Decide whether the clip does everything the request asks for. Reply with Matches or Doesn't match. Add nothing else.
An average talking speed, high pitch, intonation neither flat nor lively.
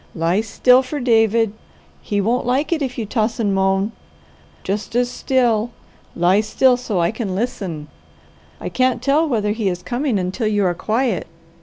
Matches